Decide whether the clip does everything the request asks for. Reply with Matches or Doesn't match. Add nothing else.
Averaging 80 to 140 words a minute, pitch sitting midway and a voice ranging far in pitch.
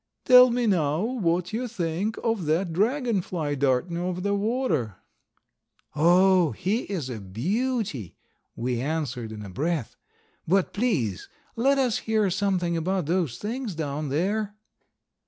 Matches